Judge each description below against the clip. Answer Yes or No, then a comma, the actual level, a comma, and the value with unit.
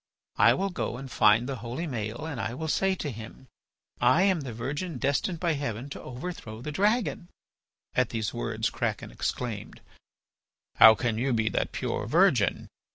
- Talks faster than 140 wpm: Yes, average, 170 wpm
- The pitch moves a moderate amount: No, wide, 6.4 semitones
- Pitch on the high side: No, low, 130 Hz